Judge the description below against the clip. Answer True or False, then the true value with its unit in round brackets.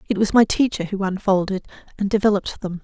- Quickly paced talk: False (190 wpm)